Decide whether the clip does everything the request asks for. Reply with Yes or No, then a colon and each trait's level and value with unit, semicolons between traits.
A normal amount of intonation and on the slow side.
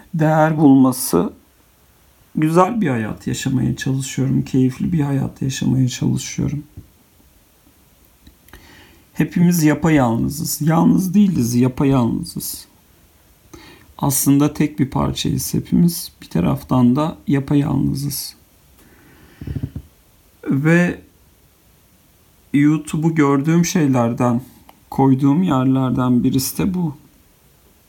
Yes: average, 4.8 semitones; slow, 80 wpm